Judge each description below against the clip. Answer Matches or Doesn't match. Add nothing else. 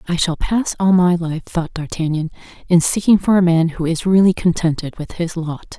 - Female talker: Matches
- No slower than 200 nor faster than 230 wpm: Matches